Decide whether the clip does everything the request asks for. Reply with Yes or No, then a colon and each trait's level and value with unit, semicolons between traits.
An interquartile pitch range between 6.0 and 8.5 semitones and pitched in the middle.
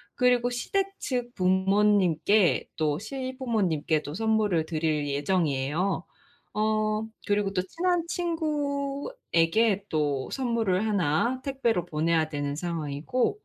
No: wide, 7.5 semitones; high, 205 Hz